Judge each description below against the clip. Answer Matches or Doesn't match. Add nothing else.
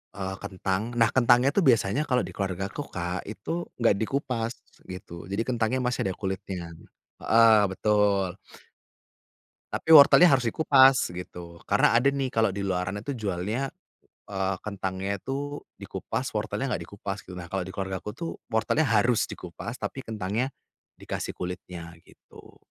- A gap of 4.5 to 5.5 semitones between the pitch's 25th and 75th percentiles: Matches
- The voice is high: Doesn't match